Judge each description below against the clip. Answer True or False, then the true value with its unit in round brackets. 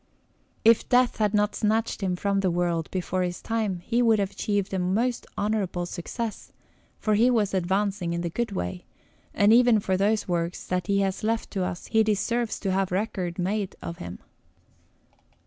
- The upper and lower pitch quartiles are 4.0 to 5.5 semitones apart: False (3.3 semitones)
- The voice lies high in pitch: True (200 Hz)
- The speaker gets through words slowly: False (180 wpm)